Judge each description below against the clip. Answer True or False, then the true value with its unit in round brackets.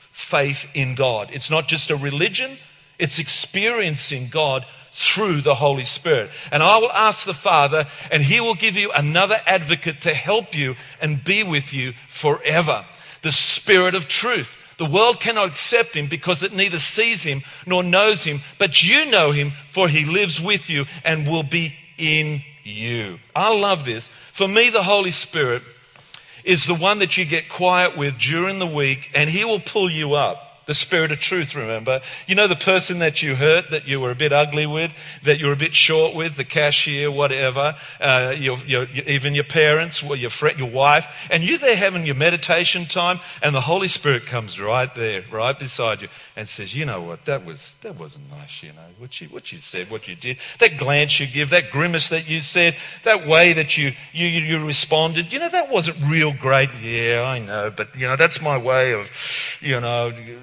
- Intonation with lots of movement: False (4.1 semitones)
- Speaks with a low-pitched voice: False (150 Hz)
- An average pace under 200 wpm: False (205 wpm)